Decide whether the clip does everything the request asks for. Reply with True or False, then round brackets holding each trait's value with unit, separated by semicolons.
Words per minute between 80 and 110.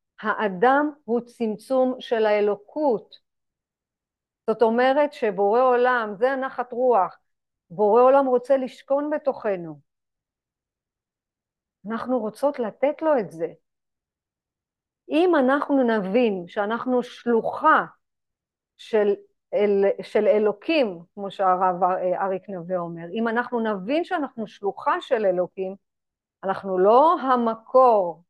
True (100 wpm)